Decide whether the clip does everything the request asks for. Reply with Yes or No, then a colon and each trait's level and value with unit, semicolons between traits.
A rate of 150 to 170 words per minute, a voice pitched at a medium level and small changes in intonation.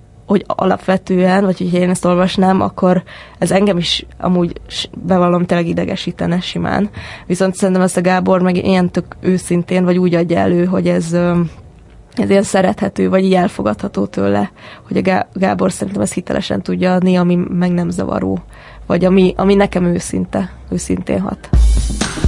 Yes: fast, 155 wpm; medium, 180 Hz; narrow, 1.2 semitones